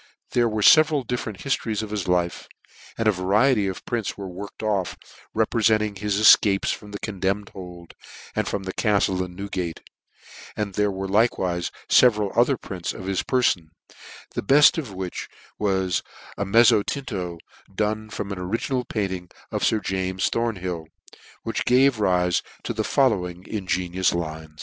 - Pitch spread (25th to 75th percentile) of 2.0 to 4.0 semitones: Yes, average, 3.2 semitones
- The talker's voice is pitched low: Yes, low, 100 Hz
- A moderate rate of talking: Yes, average, 155 wpm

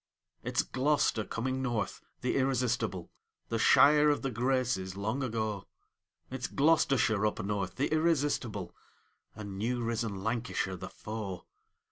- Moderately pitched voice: No, low, 115 Hz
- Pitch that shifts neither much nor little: Yes, average, 4.4 semitones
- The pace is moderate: No, slow, 125 wpm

